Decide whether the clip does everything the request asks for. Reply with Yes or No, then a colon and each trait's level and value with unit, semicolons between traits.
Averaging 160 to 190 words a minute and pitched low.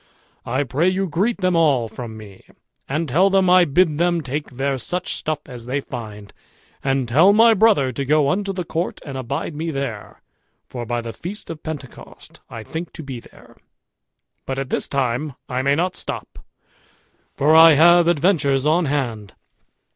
No: average, 175 wpm; medium, 145 Hz